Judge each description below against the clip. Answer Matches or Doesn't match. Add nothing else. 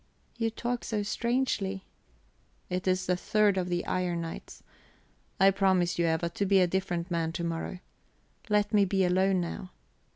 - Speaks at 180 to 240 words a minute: Doesn't match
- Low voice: Doesn't match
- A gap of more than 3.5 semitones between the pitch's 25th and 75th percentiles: Doesn't match